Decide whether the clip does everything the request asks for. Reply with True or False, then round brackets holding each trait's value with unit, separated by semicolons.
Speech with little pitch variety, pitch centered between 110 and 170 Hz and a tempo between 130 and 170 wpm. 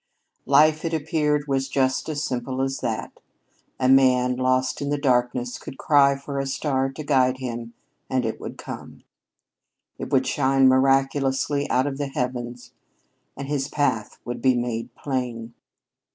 True (1.9 semitones; 135 Hz; 155 wpm)